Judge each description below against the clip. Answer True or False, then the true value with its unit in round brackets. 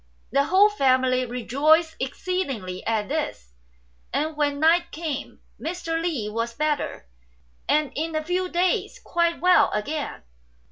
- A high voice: True (305 Hz)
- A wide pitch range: False (4.8 semitones)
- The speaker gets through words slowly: True (130 wpm)